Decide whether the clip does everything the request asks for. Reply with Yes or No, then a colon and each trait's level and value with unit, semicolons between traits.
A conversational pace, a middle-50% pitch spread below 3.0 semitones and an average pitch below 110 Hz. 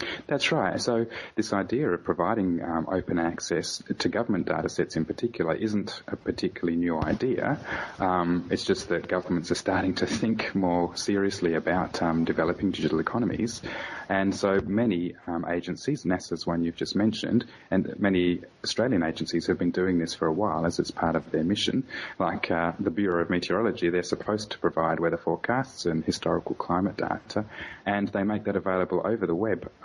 Yes: average, 175 wpm; narrow, 2.5 semitones; very low, 90 Hz